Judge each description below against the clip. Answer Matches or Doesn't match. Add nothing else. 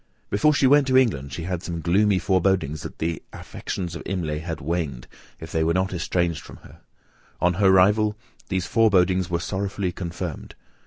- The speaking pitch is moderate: Doesn't match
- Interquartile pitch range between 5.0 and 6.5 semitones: Doesn't match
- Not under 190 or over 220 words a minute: Doesn't match